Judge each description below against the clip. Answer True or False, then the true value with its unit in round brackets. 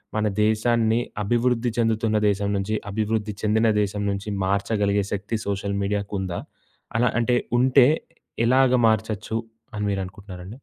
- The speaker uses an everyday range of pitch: False (2.2 semitones)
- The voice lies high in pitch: False (105 Hz)